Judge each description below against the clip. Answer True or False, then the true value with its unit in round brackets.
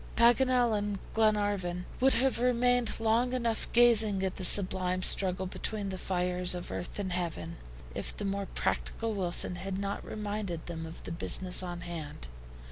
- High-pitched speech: True (195 Hz)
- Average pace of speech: True (160 wpm)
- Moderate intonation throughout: True (3.8 semitones)